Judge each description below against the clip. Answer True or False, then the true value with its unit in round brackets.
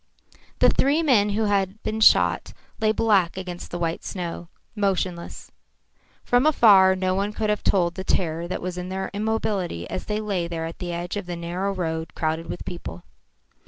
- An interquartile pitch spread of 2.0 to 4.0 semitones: True (3.4 semitones)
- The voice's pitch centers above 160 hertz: True (190 Hz)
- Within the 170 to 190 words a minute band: True (185 wpm)